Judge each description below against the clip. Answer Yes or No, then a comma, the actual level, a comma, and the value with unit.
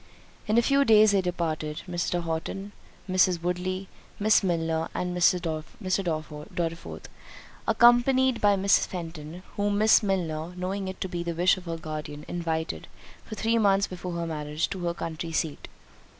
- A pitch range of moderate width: Yes, average, 3.3 semitones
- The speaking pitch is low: No, medium, 180 Hz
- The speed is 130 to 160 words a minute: Yes, average, 155 wpm